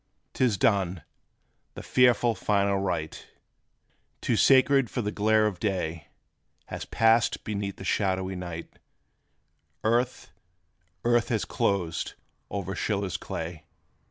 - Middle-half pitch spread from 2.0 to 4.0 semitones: Yes, average, 3.7 semitones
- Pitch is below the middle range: Yes, low, 100 Hz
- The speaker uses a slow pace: Yes, slow, 115 wpm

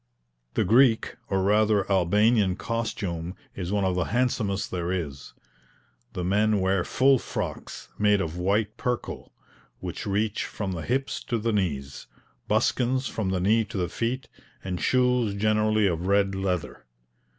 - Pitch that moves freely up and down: No, average, 3.3 semitones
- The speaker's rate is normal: Yes, average, 150 wpm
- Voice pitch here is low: Yes, low, 100 Hz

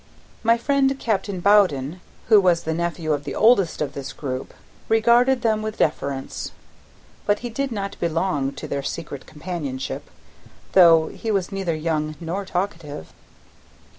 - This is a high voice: No, medium, 175 Hz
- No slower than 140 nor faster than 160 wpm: Yes, average, 145 wpm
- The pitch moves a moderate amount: No, wide, 5.9 semitones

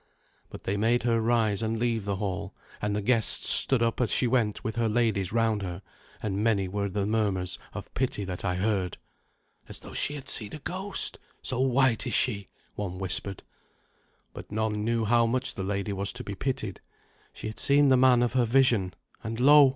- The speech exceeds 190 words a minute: Yes, average, 200 wpm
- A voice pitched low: Yes, low, 110 Hz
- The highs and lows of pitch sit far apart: No, average, 3.4 semitones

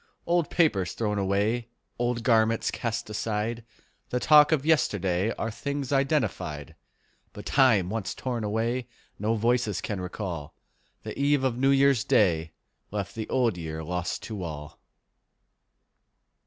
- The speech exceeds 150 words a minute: No, slow, 135 wpm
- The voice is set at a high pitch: No, low, 110 Hz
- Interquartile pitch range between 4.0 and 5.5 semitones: Yes, average, 4.8 semitones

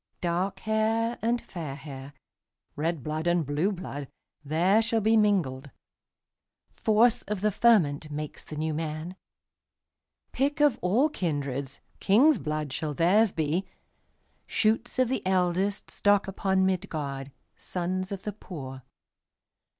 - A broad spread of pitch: Yes, wide, 5.8 semitones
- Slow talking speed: Yes, slow, 100 wpm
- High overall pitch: No, medium, 180 Hz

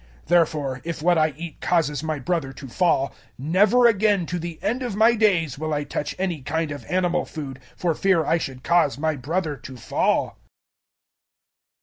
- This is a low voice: No, medium, 165 Hz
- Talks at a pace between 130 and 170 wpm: No, average, 185 wpm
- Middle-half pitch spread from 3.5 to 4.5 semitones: Yes, average, 3.8 semitones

